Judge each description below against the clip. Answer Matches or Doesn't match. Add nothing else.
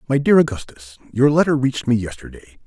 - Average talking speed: Matches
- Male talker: Matches